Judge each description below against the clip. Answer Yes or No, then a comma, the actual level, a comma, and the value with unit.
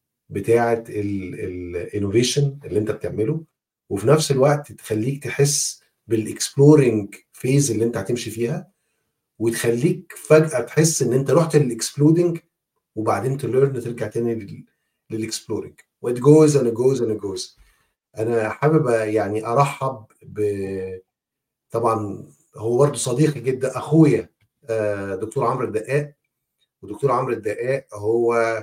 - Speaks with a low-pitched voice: Yes, low, 120 Hz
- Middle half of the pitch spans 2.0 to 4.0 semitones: No, average, 4.8 semitones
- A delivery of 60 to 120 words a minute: Yes, average, 110 wpm